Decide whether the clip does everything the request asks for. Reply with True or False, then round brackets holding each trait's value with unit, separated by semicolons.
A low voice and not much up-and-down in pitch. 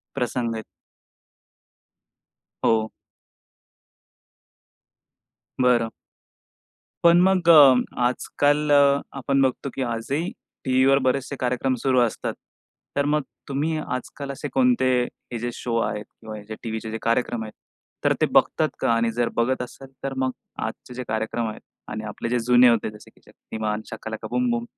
False (125 Hz; 3.5 semitones)